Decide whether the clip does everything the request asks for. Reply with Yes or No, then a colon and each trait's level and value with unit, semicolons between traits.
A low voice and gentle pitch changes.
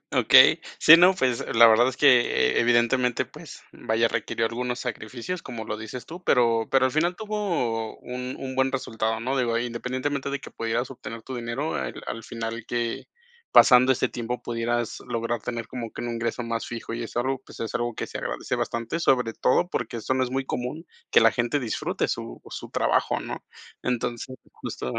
Yes: low, 120 Hz; narrow, 2.2 semitones